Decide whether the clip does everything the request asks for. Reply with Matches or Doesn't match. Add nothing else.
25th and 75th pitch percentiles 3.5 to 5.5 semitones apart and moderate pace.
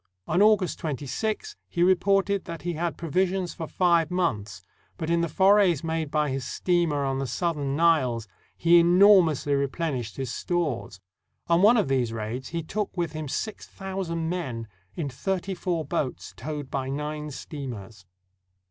Matches